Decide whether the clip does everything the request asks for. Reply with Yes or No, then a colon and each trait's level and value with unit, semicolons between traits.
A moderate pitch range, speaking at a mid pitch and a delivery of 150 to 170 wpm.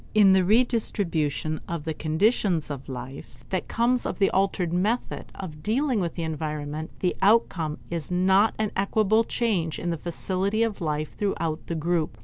Yes: average, 4.9 semitones; medium, 180 Hz; average, 165 wpm